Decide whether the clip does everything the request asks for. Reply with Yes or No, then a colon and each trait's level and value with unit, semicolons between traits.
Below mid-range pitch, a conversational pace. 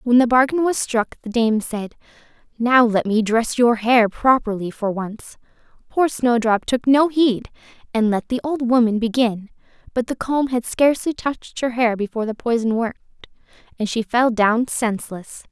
No: high, 235 Hz; average, 175 wpm